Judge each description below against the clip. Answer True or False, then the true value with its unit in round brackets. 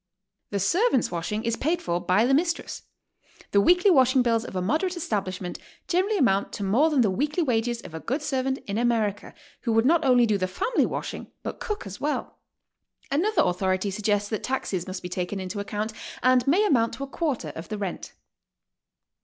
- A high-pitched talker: True (230 Hz)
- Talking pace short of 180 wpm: False (195 wpm)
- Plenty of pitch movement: True (6.6 semitones)